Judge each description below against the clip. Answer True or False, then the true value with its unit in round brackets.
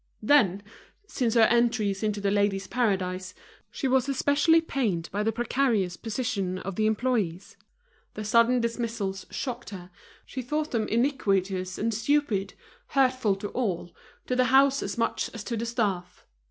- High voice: True (225 Hz)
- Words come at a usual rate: True (155 wpm)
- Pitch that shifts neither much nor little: True (4.3 semitones)